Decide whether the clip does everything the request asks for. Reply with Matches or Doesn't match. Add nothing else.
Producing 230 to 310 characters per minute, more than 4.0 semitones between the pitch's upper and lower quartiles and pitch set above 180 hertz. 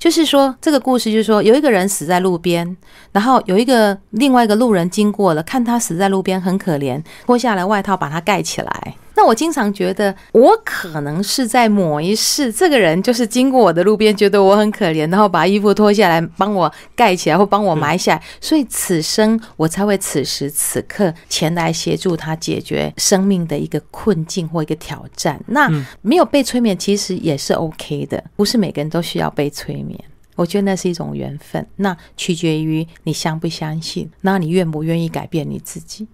Matches